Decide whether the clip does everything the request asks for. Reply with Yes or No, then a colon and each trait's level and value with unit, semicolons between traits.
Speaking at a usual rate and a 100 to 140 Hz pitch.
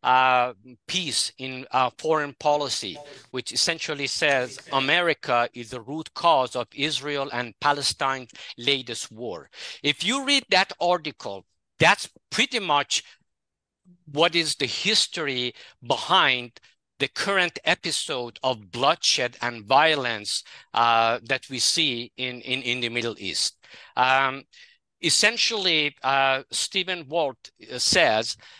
No: slow, 115 wpm; low, 135 Hz